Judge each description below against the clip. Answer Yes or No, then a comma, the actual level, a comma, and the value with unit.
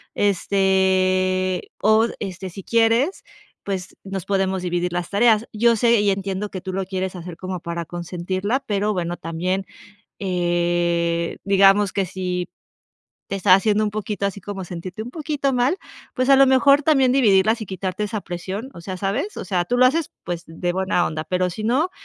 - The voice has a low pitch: No, high, 195 Hz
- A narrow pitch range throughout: No, average, 3.2 semitones